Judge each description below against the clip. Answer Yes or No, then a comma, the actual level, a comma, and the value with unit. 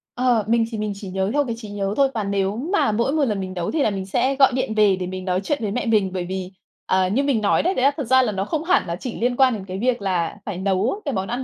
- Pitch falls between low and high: No, high, 215 Hz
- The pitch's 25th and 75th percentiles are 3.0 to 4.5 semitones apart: No, average, 5.0 semitones